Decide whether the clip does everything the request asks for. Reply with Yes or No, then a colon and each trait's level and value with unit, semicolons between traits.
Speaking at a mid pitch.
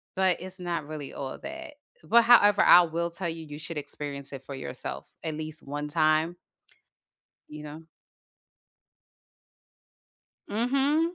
Yes: medium, 165 Hz